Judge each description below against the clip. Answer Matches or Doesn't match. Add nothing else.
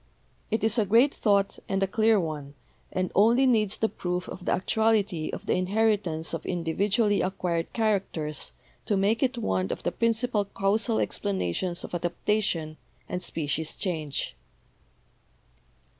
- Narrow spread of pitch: Doesn't match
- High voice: Matches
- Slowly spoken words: Doesn't match